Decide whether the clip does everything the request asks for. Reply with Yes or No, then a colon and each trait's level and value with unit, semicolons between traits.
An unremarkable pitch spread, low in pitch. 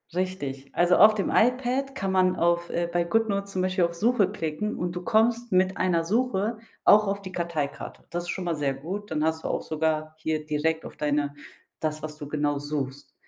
No: average, 4.4 semitones; medium, 175 Hz